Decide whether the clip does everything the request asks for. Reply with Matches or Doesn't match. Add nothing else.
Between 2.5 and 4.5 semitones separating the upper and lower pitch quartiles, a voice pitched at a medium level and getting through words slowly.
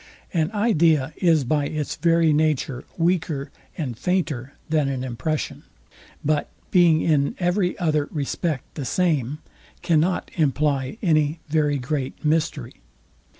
Matches